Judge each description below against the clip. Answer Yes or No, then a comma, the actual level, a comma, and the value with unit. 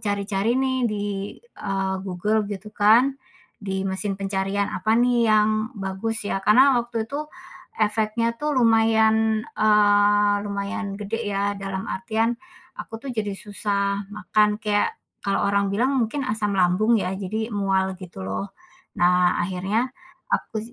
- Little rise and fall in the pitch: Yes, narrow, 2.2 semitones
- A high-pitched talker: Yes, high, 210 Hz